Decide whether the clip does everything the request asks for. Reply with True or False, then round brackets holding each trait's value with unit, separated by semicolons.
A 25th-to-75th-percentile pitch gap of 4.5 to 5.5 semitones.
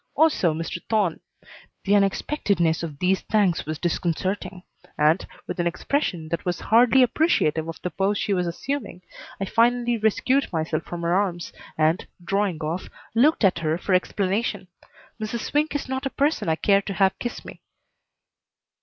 True (5.0 semitones)